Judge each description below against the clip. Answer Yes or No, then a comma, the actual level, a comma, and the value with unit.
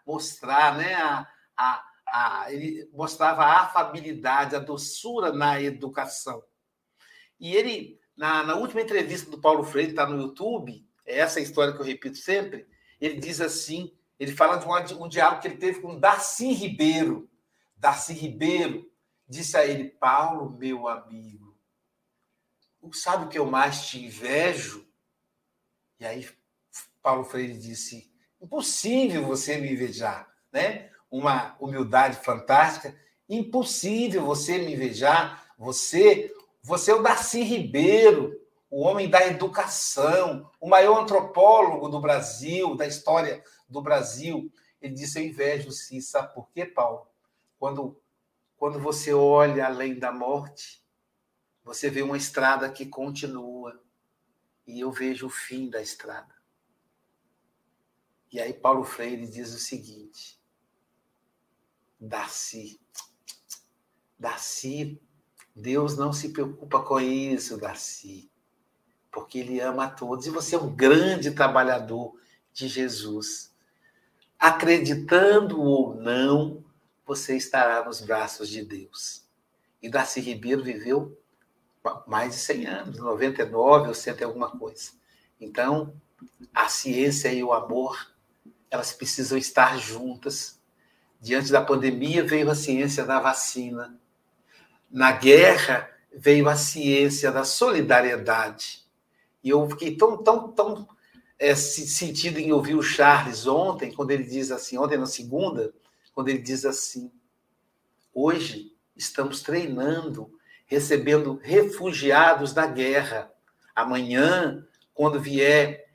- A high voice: No, medium, 145 Hz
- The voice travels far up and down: No, average, 4.2 semitones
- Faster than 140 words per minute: No, average, 125 wpm